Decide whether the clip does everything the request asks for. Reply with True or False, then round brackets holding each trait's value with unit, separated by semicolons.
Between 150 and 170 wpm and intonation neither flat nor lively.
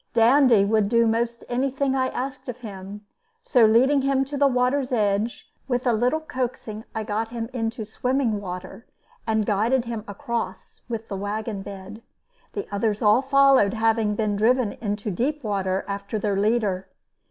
True (165 wpm; 3.5 semitones)